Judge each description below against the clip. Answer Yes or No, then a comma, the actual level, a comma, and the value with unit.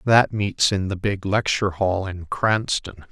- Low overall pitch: Yes, low, 100 Hz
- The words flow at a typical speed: Yes, average, 175 wpm